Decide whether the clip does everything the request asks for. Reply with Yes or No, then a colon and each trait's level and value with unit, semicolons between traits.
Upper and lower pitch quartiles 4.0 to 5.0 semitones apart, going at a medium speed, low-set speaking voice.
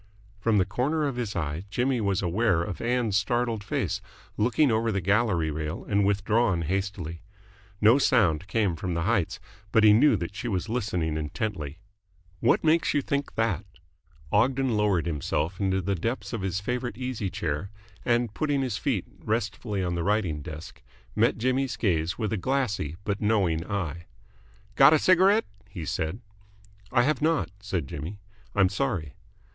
No: wide, 5.4 semitones; average, 165 wpm; low, 105 Hz